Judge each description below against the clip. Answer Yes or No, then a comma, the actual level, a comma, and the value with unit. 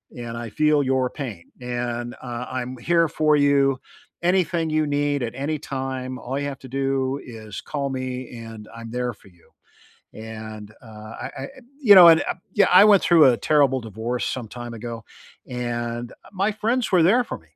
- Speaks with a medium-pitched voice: No, low, 130 Hz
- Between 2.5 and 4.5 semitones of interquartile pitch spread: Yes, average, 4.1 semitones